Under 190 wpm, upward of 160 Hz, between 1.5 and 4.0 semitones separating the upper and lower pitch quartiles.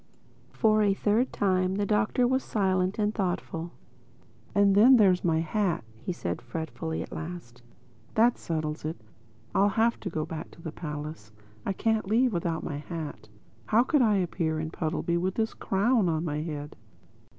No: average, 170 wpm; medium, 185 Hz; average, 4.8 semitones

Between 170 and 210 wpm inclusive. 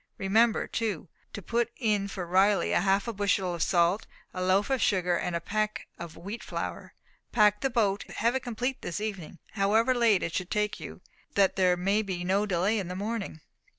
Yes: average, 200 wpm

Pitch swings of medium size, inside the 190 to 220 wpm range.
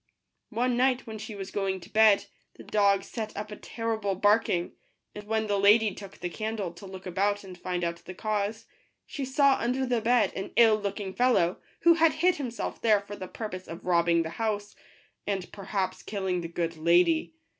Yes: average, 3.3 semitones; average, 200 wpm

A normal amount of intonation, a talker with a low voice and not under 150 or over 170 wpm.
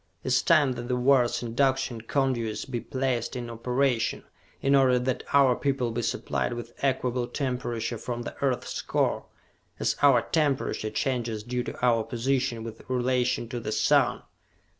No: narrow, 2.0 semitones; low, 125 Hz; average, 160 wpm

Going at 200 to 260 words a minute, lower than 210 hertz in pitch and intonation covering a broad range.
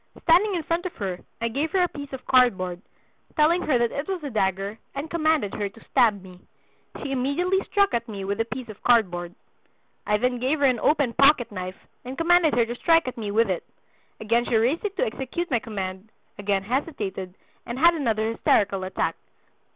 No: fast, 205 wpm; high, 240 Hz; wide, 6.9 semitones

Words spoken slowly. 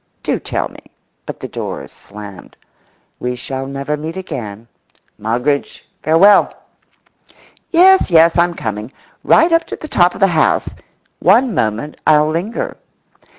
Yes: slow, 125 wpm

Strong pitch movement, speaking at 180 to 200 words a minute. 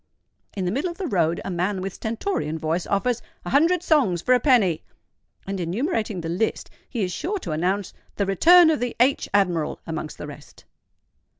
Yes: wide, 7.5 semitones; average, 185 wpm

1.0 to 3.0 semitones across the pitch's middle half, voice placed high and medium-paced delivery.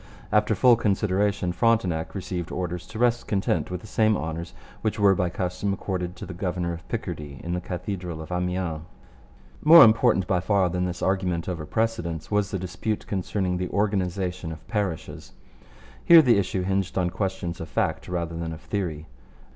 No: average, 2.7 semitones; very low, 90 Hz; average, 170 wpm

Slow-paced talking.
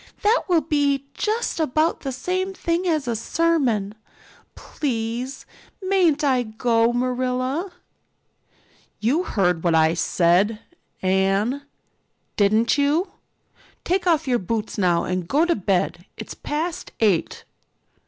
Yes: slow, 120 wpm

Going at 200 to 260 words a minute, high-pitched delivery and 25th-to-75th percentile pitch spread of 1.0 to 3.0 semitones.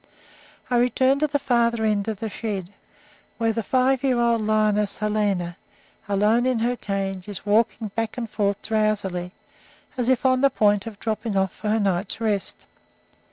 No: average, 170 wpm; high, 215 Hz; average, 2.7 semitones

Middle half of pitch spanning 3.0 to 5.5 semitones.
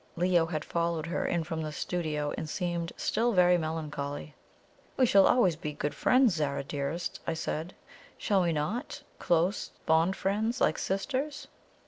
Yes: average, 3.7 semitones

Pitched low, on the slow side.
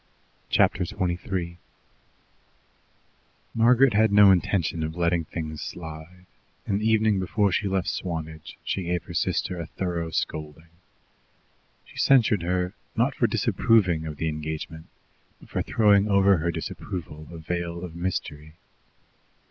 Yes: very low, 85 Hz; slow, 130 wpm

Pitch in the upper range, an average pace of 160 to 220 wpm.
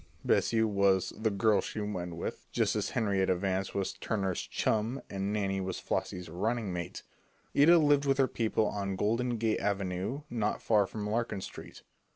No: low, 105 Hz; average, 170 wpm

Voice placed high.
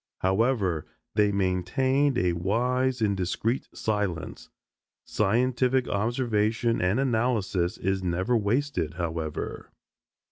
No: low, 105 Hz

